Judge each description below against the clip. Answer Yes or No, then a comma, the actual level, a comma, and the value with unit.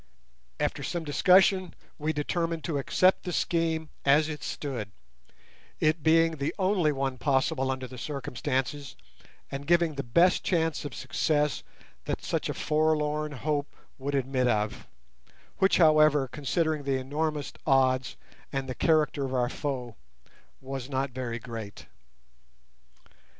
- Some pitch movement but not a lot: Yes, average, 3.2 semitones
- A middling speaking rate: No, slow, 130 wpm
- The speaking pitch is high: No, medium, 145 Hz